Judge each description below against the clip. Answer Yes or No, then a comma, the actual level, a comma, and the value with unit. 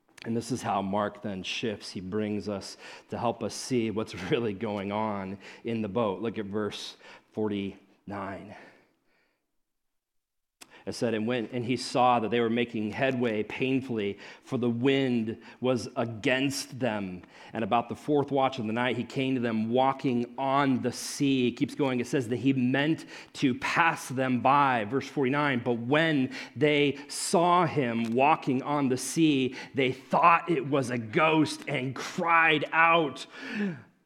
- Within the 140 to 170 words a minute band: Yes, average, 160 wpm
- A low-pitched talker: Yes, low, 125 Hz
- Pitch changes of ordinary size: Yes, average, 3.9 semitones